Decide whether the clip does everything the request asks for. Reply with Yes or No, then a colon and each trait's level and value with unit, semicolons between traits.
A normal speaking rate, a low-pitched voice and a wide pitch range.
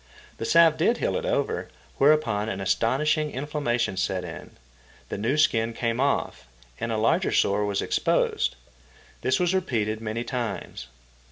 Yes: average, 150 wpm; low, 120 Hz; wide, 6.0 semitones